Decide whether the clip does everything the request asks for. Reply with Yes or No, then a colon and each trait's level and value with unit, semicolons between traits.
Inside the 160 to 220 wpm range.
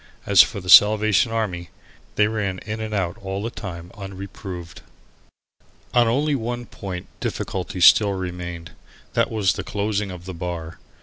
No: average, 150 wpm